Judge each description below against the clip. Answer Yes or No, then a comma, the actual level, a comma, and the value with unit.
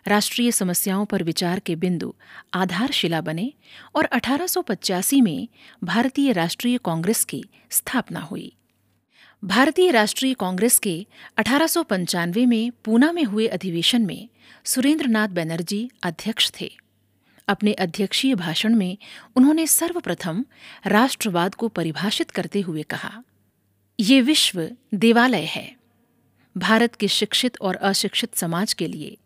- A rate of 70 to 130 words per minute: Yes, average, 115 wpm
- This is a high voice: Yes, high, 215 Hz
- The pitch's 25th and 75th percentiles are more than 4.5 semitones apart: Yes, average, 5.3 semitones